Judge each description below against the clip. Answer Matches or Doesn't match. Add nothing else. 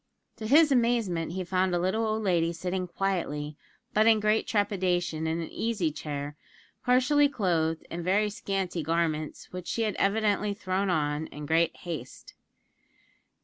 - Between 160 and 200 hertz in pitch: Matches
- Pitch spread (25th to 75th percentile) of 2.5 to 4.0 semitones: Doesn't match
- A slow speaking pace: Doesn't match